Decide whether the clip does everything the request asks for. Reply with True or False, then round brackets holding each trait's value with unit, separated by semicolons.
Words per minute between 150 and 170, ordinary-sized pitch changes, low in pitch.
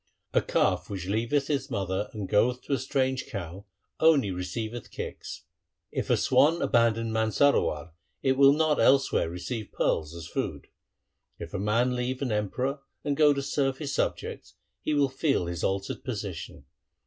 False (160 wpm; 5.7 semitones; 120 Hz)